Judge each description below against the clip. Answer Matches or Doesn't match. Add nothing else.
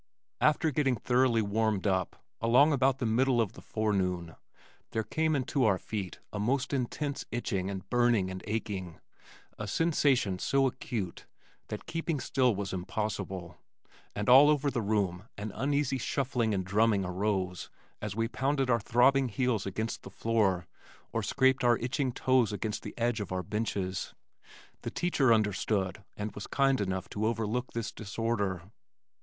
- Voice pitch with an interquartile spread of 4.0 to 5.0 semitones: Matches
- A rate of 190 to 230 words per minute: Doesn't match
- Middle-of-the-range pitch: Doesn't match